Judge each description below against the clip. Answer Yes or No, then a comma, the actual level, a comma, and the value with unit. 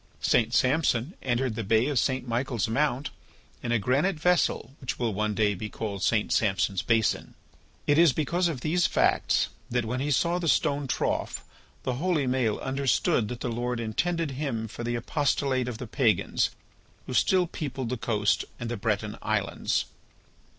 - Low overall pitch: Yes, low, 125 Hz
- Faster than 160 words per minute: Yes, average, 170 wpm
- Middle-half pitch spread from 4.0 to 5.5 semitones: Yes, average, 4.3 semitones